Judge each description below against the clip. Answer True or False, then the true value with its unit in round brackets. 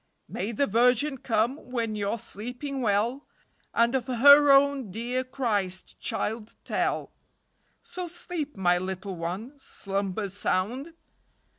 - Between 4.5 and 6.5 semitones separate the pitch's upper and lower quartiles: True (5.2 semitones)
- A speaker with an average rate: False (115 wpm)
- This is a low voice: False (235 Hz)